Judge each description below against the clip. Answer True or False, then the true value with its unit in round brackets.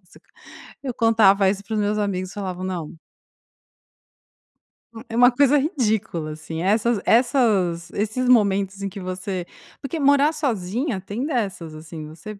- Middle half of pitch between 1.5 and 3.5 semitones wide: False (4.8 semitones)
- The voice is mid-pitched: False (205 Hz)